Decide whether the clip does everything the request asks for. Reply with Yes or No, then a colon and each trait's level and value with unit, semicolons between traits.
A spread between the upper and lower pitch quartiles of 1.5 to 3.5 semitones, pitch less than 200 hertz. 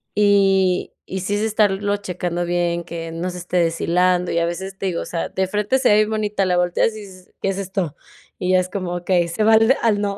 Yes: narrow, 2.6 semitones; medium, 185 Hz